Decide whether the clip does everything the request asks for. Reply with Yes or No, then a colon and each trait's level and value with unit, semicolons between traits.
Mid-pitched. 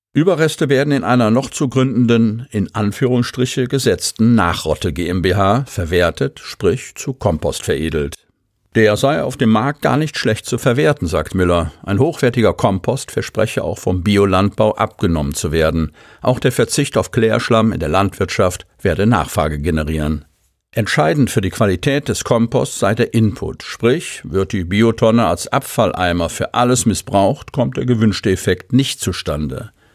No: low, 110 Hz